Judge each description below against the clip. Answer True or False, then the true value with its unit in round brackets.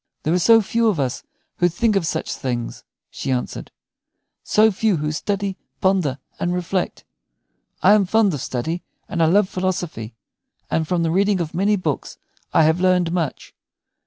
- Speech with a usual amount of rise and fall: True (3.7 semitones)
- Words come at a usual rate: True (170 wpm)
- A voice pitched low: False (180 Hz)